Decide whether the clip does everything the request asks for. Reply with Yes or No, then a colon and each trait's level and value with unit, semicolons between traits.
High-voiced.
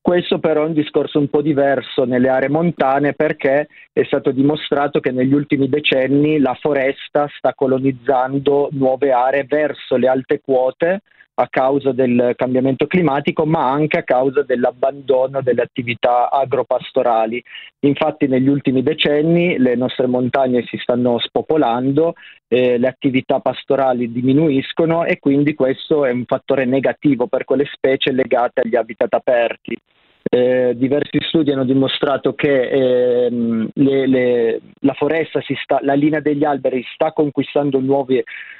No: low, 135 Hz